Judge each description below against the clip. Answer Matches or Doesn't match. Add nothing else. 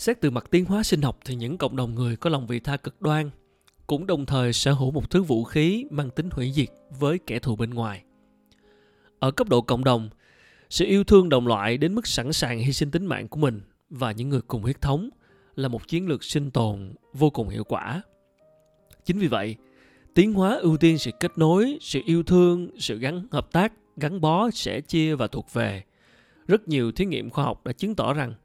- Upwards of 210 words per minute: Matches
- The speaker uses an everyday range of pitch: Doesn't match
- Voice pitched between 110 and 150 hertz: Matches